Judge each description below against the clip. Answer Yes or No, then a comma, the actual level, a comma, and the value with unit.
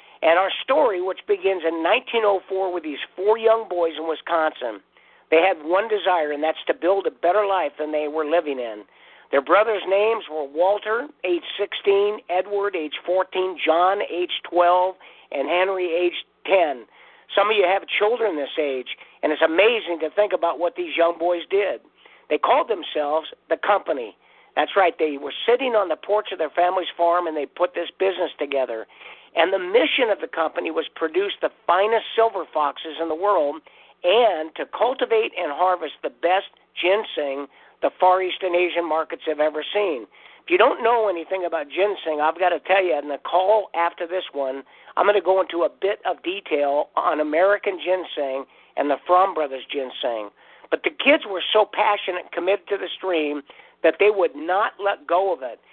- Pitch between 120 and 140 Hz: No, medium, 180 Hz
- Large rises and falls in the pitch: No, average, 4.0 semitones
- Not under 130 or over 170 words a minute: No, average, 185 wpm